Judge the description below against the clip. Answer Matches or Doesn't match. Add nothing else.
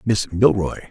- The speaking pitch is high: Doesn't match